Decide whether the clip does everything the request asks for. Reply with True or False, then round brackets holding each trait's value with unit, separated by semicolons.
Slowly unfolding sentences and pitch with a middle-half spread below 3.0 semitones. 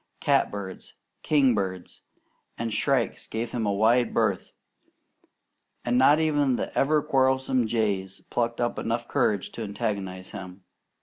False (130 wpm; 4.6 semitones)